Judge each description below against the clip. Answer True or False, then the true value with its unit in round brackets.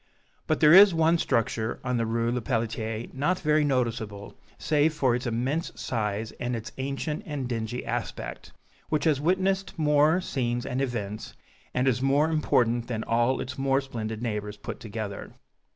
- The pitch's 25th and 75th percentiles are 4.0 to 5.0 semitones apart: True (4.6 semitones)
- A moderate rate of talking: True (160 wpm)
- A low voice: True (125 Hz)